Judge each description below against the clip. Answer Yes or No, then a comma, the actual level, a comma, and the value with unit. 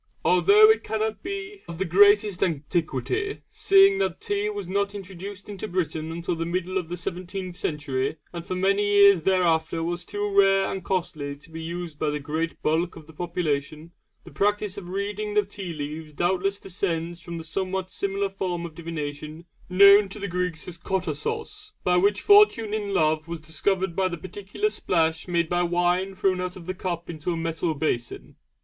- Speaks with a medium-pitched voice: Yes, medium, 180 Hz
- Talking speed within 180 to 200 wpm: Yes, average, 185 wpm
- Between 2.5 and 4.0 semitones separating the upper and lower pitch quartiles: Yes, average, 3.4 semitones